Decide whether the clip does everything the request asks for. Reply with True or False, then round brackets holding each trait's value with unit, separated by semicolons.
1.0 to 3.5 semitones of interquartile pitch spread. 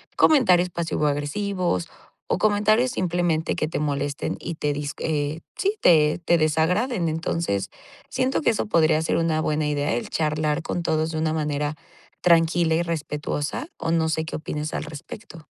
True (2.6 semitones)